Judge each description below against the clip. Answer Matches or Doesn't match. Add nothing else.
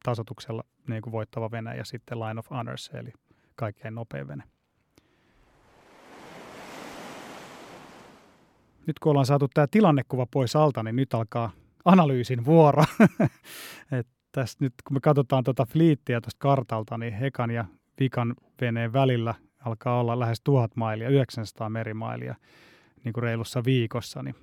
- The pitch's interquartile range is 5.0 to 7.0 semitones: Doesn't match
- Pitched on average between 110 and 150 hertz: Matches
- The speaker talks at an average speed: Matches